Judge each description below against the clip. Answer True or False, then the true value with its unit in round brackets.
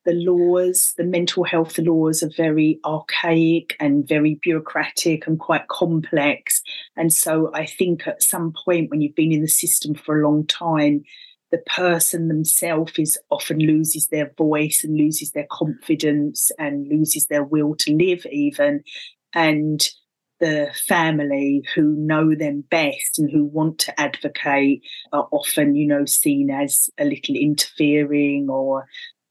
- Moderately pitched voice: True (155 Hz)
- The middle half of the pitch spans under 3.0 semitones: True (2.5 semitones)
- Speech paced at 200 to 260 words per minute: False (145 wpm)